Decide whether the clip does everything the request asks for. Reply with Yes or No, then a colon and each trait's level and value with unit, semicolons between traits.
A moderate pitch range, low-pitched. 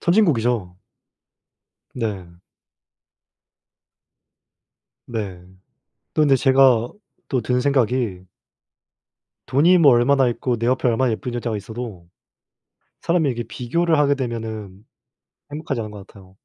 Yes: average, 3.8 semitones; low, 120 Hz